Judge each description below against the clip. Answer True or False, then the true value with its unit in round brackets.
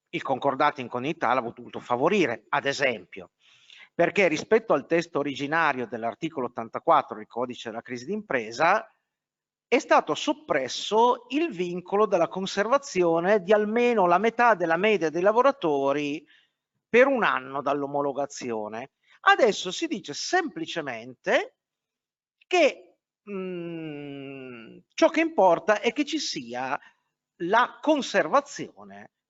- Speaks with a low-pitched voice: False (175 Hz)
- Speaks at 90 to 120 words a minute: True (115 wpm)